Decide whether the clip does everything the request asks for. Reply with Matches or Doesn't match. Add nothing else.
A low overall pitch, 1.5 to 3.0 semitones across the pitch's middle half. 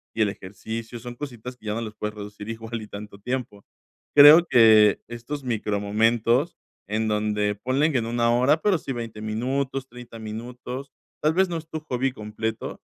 Doesn't match